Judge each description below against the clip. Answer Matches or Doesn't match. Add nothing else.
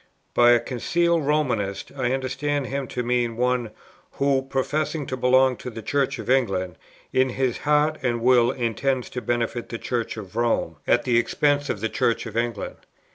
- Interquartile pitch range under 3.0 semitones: Matches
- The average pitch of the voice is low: Matches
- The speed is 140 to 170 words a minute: Doesn't match